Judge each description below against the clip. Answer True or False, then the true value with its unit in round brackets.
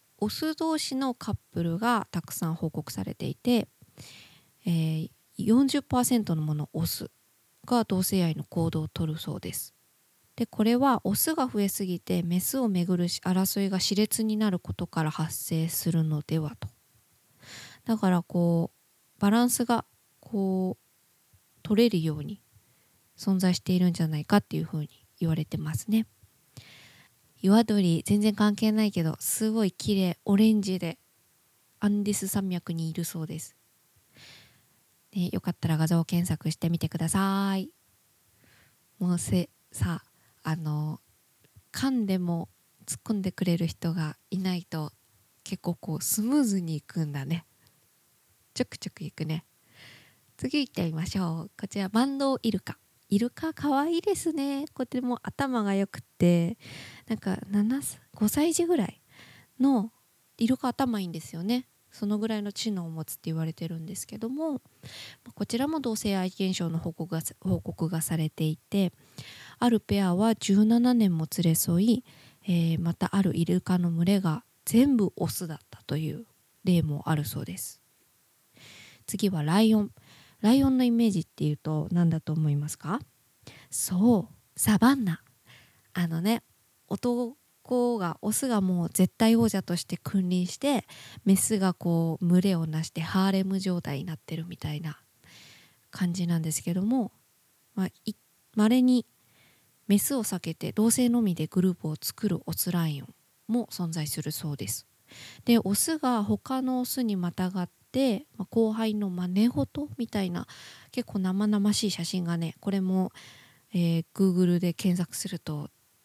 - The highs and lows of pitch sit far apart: False (5.0 semitones)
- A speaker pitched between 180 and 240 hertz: True (185 Hz)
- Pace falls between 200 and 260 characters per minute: False (285 characters per minute)